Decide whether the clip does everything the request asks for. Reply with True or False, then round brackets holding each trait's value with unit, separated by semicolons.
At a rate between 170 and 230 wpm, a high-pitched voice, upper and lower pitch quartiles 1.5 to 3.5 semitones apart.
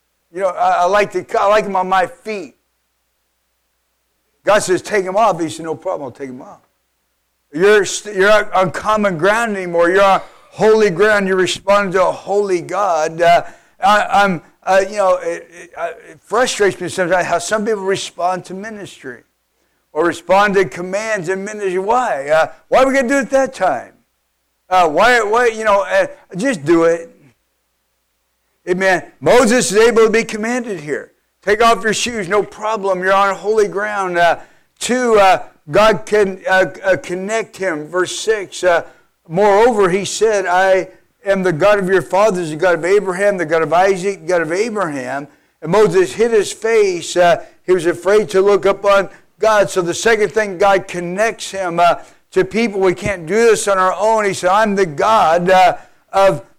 True (185 wpm; 195 Hz; 3.2 semitones)